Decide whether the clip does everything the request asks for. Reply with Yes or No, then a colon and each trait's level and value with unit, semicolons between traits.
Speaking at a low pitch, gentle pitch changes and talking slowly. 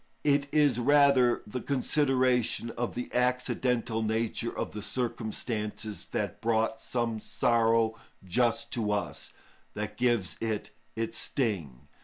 Yes: low, 115 Hz; narrow, 2.3 semitones; slow, 120 wpm